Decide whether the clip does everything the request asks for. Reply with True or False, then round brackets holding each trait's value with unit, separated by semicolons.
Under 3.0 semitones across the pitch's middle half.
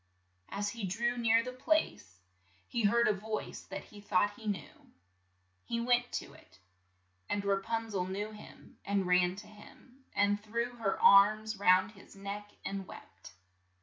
True (2.6 semitones)